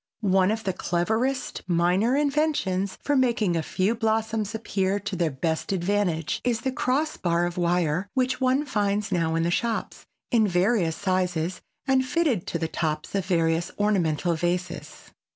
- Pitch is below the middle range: No, high, 190 Hz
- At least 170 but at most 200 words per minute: No, average, 160 wpm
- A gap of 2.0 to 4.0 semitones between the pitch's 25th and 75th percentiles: No, average, 4.8 semitones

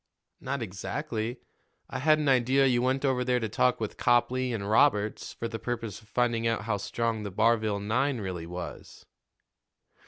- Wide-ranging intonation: No, average, 3.3 semitones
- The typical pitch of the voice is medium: No, low, 115 Hz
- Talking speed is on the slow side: No, average, 175 wpm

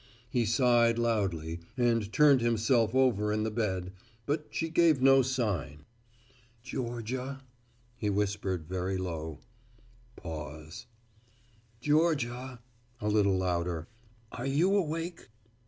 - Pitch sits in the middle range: No, low, 115 Hz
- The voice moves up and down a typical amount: No, wide, 5.9 semitones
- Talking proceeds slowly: Yes, slow, 105 wpm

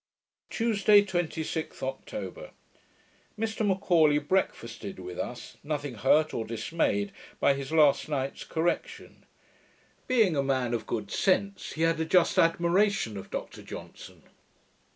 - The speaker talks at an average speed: No, slow, 125 wpm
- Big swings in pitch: Yes, wide, 6.4 semitones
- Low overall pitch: No, medium, 160 Hz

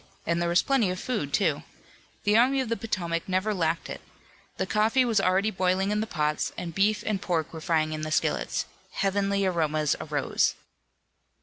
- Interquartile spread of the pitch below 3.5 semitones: No, average, 4.3 semitones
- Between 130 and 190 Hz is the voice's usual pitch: Yes, medium, 185 Hz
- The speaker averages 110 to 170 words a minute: No, average, 185 wpm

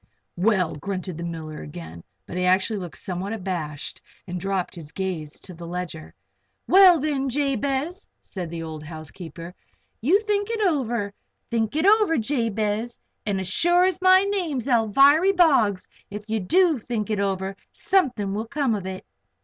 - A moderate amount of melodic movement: No, wide, 8.2 semitones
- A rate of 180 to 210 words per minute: No, average, 165 wpm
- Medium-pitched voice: No, high, 210 Hz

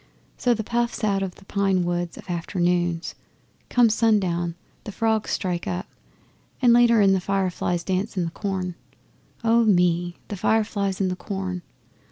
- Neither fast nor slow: Yes, average, 160 wpm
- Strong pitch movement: No, average, 3.5 semitones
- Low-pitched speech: No, high, 195 Hz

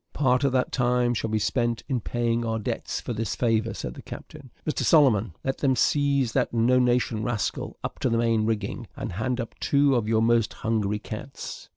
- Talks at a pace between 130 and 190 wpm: No, fast, 205 wpm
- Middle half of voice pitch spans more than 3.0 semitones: No, narrow, 2.4 semitones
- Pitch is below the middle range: Yes, low, 120 Hz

